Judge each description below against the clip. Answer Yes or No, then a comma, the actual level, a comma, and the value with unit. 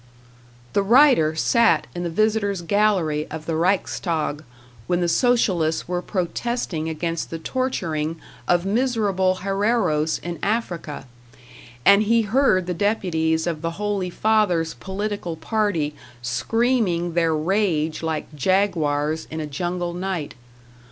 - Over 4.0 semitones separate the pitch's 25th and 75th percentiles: Yes, average, 4.4 semitones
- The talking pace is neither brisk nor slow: No, slow, 125 wpm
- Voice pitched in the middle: Yes, medium, 175 Hz